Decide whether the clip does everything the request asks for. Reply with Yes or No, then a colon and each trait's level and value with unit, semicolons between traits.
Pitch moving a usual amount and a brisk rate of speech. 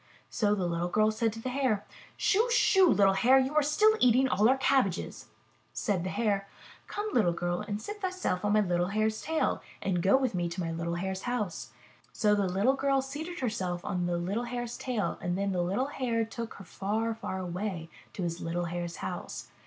No: wide, 6.0 semitones; fast, 210 wpm